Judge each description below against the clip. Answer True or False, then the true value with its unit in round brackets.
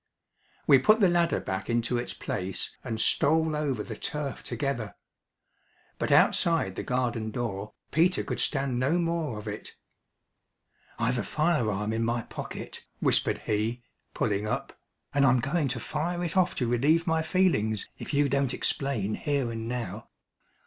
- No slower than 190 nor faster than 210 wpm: False (160 wpm)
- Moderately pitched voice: False (125 Hz)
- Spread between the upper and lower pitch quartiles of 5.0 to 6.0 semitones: True (5.6 semitones)